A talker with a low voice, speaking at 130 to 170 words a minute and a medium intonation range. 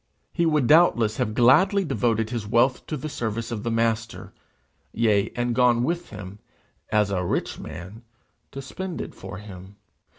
Yes: low, 115 Hz; average, 165 wpm; average, 4.2 semitones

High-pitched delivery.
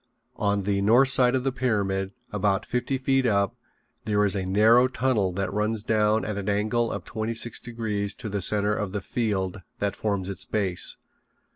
No: low, 105 Hz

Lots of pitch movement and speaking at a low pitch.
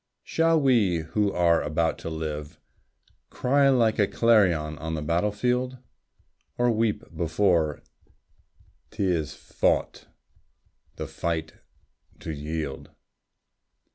Yes: wide, 6.4 semitones; very low, 85 Hz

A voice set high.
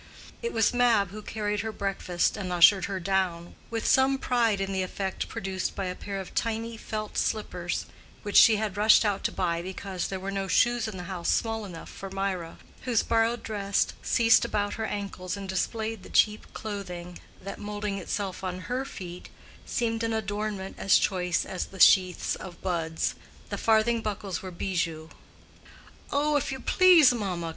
Yes: high, 200 Hz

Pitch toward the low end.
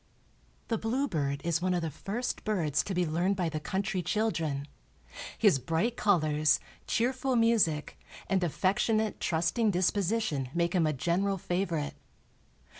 No: medium, 180 Hz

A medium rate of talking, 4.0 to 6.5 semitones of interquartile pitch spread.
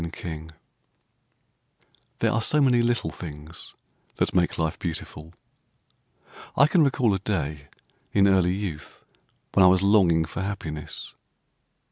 No: slow, 125 wpm; average, 4.5 semitones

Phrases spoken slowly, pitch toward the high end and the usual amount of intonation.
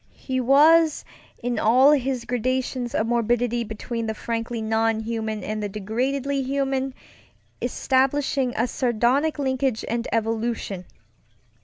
Yes: slow, 120 wpm; high, 240 Hz; average, 3.0 semitones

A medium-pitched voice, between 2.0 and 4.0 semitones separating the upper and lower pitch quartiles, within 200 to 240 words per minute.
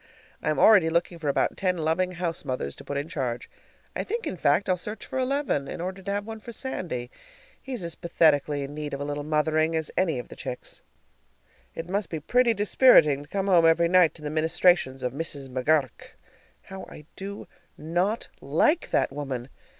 No: medium, 165 Hz; average, 4.7 semitones; fast, 205 wpm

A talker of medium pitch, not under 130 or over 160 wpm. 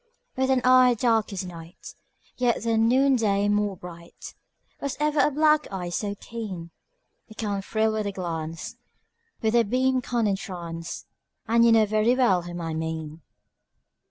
No: high, 215 Hz; average, 155 wpm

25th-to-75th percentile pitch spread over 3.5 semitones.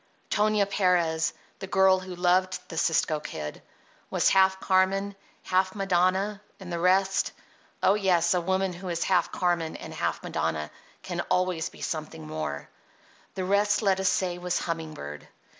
No: narrow, 2.4 semitones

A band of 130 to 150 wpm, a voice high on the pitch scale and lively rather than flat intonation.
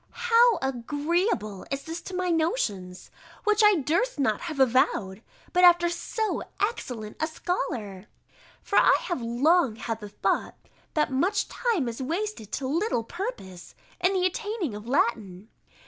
Yes: average, 145 wpm; very high, 300 Hz; wide, 8.3 semitones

